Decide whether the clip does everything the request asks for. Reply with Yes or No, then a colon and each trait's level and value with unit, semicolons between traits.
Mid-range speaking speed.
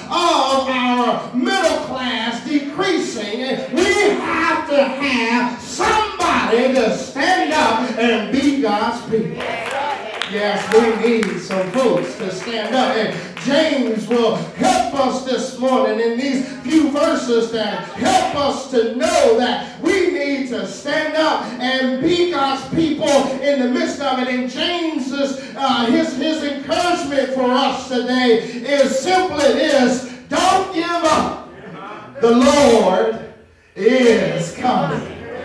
No: slow, 125 wpm